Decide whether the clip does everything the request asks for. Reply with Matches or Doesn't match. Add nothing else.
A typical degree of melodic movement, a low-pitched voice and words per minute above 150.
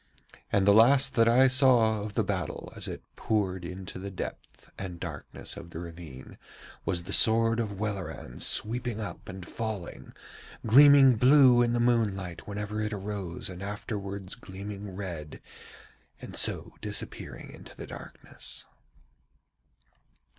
Doesn't match